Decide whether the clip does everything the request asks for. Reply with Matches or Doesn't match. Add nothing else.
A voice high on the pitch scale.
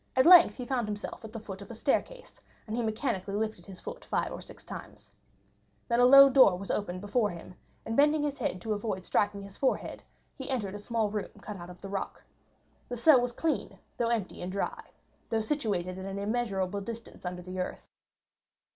Matches